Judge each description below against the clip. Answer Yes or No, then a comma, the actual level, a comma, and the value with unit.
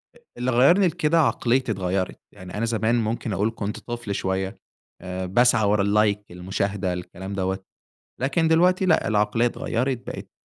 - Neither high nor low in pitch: No, low, 110 Hz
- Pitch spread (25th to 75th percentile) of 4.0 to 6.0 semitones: Yes, average, 4.6 semitones